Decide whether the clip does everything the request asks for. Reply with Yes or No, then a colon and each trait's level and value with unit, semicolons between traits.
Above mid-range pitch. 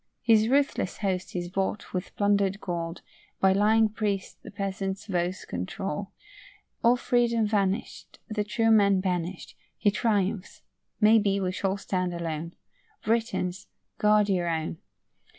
Yes: high, 195 Hz